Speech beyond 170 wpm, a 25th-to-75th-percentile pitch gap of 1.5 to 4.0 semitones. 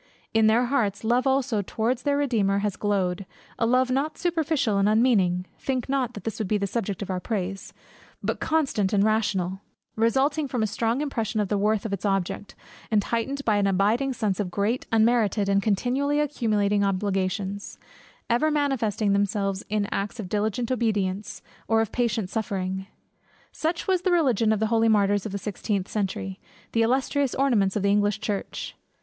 Yes: average, 180 wpm; average, 3.7 semitones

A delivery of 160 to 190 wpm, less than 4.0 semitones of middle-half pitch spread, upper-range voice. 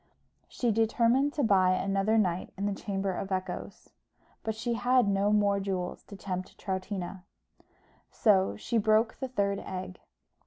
No: average, 150 wpm; average, 2.8 semitones; high, 200 Hz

